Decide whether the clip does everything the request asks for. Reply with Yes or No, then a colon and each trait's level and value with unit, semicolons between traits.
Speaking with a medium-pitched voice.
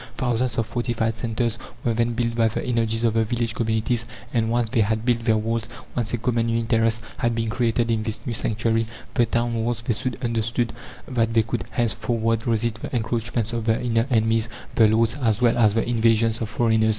No: low, 115 Hz